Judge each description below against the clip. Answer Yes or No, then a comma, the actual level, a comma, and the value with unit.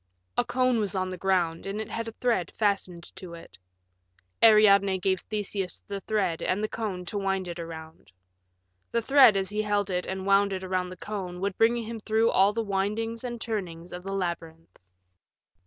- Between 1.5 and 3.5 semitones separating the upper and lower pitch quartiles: Yes, average, 2.9 semitones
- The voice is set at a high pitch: Yes, high, 195 Hz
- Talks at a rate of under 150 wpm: No, average, 190 wpm